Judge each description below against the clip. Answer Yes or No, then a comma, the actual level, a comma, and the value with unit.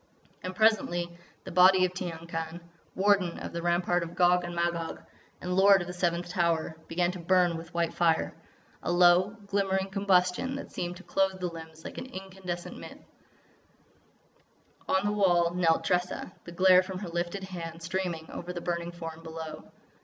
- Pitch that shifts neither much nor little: No, narrow, 1.8 semitones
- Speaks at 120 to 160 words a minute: No, average, 170 wpm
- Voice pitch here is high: No, medium, 175 Hz